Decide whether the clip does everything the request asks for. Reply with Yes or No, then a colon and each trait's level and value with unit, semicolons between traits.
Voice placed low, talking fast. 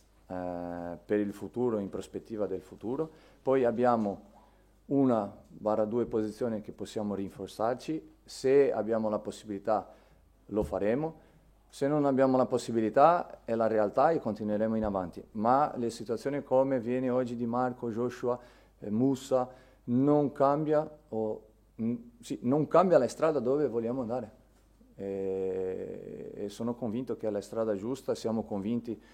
No: low, 115 Hz; average, 140 wpm